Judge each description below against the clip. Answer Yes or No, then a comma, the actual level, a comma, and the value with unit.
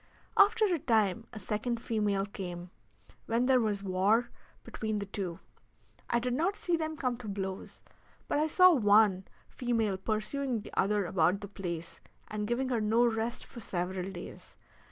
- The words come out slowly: No, average, 165 wpm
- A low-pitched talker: No, high, 215 Hz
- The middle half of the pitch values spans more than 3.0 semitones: Yes, average, 3.9 semitones